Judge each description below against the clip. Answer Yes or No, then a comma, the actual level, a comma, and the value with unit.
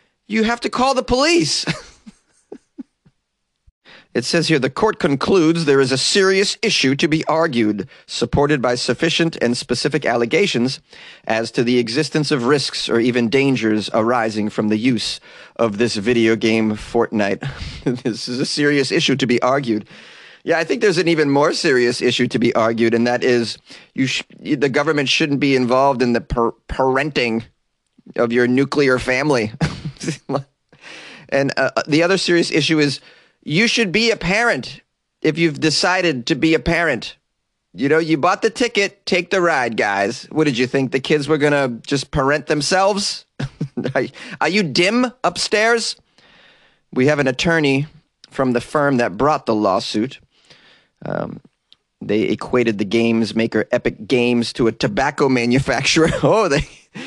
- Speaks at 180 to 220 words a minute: No, average, 160 wpm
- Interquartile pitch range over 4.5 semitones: Yes, average, 5.0 semitones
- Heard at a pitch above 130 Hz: Yes, medium, 140 Hz